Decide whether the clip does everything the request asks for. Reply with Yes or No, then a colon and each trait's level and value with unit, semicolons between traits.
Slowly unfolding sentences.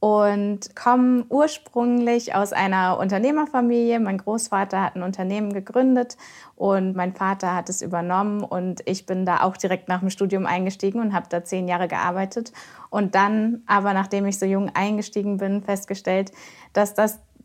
No: average, 160 wpm